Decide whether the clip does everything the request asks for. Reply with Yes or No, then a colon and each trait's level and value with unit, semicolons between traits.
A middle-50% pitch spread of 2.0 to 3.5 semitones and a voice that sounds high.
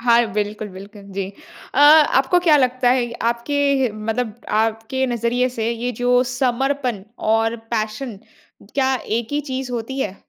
Yes: average, 2.9 semitones; high, 240 Hz